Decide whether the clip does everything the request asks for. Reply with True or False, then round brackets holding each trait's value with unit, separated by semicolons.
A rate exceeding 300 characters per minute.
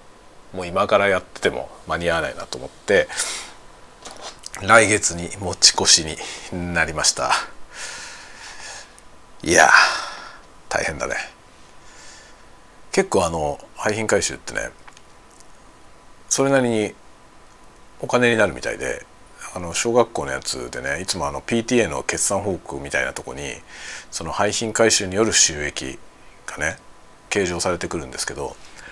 False (250 characters per minute)